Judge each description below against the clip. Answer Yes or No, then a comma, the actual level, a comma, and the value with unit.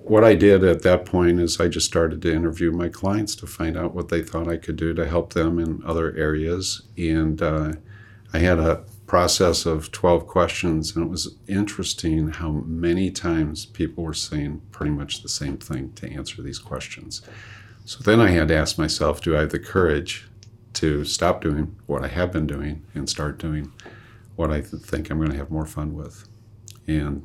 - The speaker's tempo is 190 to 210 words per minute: Yes, average, 200 wpm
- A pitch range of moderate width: Yes, average, 4.6 semitones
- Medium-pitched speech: No, very low, 85 Hz